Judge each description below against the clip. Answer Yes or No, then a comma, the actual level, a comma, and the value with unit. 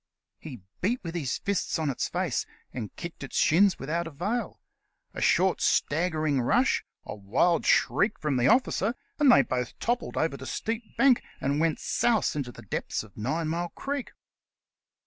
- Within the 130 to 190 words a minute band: Yes, average, 165 wpm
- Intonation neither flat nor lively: No, wide, 7.5 semitones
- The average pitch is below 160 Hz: No, medium, 165 Hz